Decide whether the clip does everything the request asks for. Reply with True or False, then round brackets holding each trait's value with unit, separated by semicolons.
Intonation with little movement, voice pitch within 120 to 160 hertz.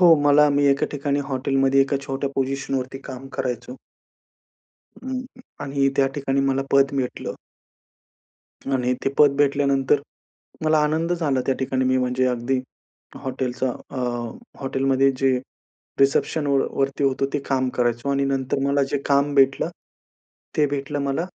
True (1.1 semitones; 135 Hz)